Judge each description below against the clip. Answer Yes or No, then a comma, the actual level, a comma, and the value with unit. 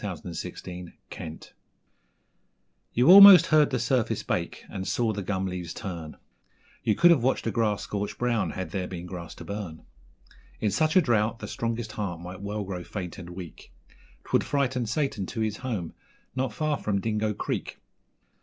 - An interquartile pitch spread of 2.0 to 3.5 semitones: No, average, 4.9 semitones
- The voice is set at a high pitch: No, low, 105 Hz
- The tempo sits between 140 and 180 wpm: Yes, average, 170 wpm